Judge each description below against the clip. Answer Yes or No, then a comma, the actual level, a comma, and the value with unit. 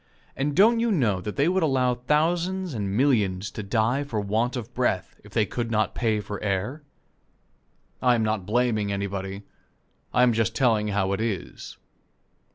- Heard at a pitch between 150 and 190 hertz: No, low, 115 Hz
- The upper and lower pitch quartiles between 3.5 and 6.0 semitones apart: Yes, average, 4.5 semitones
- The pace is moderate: Yes, average, 170 wpm